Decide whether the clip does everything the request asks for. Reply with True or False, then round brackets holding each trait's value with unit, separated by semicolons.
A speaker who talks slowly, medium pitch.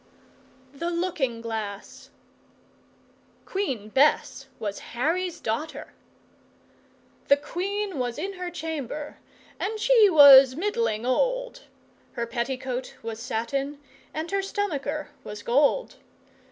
False (100 wpm; 290 Hz)